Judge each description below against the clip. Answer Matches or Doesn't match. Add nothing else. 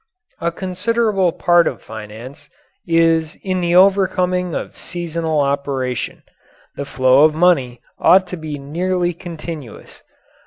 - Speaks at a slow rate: Matches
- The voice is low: Doesn't match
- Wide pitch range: Doesn't match